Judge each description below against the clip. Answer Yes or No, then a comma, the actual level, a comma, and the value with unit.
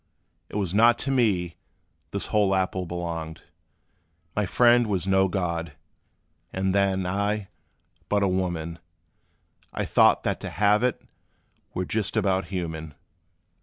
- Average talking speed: No, slow, 130 wpm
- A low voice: Yes, very low, 95 Hz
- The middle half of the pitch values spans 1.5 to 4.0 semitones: Yes, average, 2.9 semitones